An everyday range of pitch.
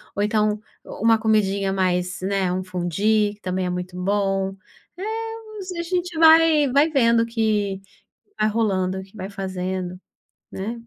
Yes: average, 3.8 semitones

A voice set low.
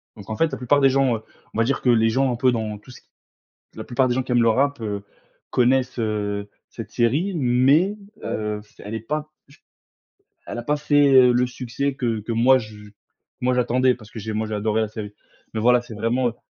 Yes: low, 120 Hz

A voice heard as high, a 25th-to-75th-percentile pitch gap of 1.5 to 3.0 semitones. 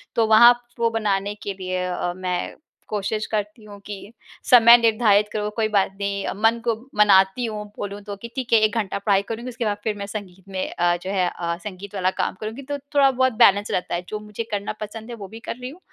Yes: high, 210 Hz; narrow, 2.6 semitones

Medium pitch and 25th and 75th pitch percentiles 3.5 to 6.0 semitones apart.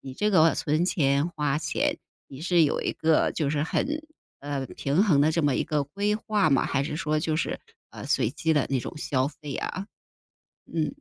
No: medium, 155 Hz; average, 3.1 semitones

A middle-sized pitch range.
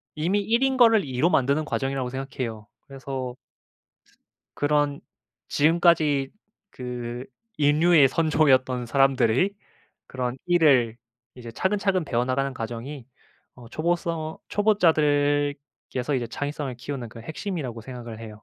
Yes: average, 4.1 semitones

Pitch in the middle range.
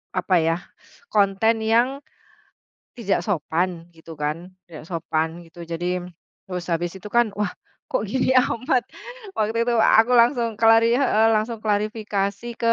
No: high, 205 Hz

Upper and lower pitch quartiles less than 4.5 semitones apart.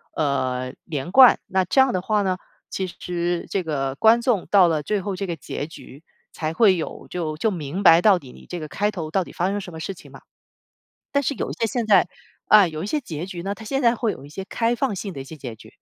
No: average, 4.9 semitones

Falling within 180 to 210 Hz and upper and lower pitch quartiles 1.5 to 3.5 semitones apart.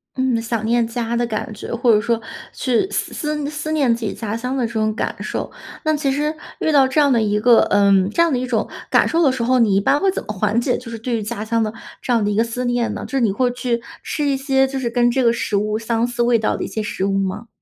No: high, 235 Hz; average, 3.1 semitones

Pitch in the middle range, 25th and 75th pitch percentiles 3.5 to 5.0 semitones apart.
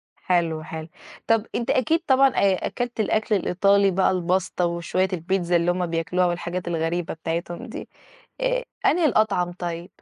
Yes: medium, 180 Hz; average, 3.9 semitones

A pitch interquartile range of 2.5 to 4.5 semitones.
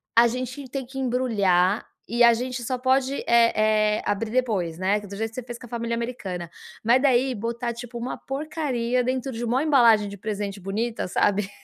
Yes: average, 3.3 semitones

